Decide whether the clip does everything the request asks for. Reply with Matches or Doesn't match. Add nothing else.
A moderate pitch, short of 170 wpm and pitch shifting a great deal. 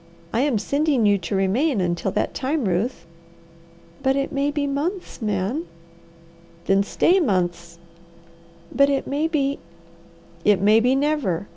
Doesn't match